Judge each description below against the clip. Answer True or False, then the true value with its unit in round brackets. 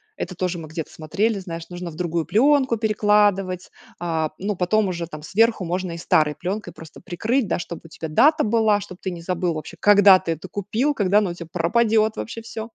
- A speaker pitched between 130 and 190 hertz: True (185 Hz)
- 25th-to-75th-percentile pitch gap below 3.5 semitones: False (4.2 semitones)